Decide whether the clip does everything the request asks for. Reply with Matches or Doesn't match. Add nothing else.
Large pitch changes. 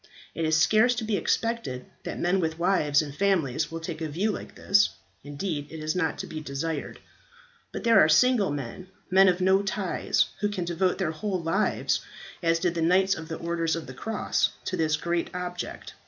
Doesn't match